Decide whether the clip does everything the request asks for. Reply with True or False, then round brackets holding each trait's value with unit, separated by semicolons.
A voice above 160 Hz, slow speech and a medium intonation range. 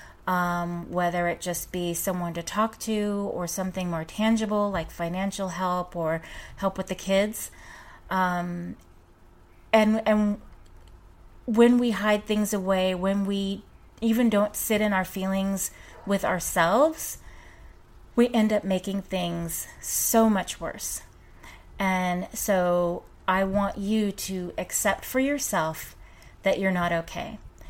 True (190 Hz; 130 wpm; 3.2 semitones)